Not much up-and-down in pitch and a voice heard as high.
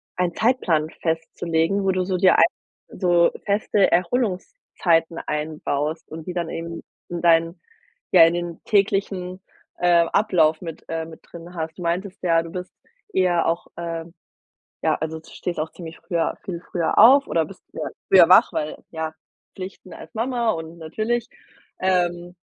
No: narrow, 2.3 semitones; medium, 175 Hz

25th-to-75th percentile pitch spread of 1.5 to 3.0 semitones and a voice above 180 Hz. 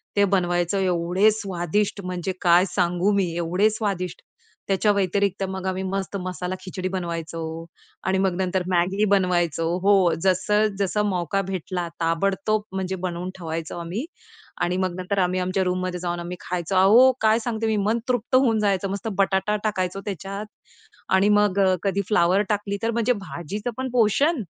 Yes: narrow, 2.4 semitones; high, 190 Hz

